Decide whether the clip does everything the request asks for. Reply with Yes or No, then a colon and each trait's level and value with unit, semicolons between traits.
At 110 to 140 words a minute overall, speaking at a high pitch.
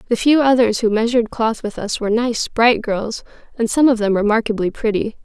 No: fast, 205 wpm; high, 225 Hz